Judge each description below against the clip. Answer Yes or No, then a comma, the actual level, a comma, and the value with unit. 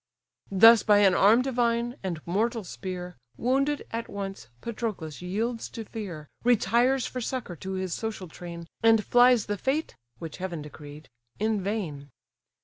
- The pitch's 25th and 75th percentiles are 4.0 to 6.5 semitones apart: Yes, average, 4.7 semitones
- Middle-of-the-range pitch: No, high, 210 Hz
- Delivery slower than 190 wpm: Yes, average, 145 wpm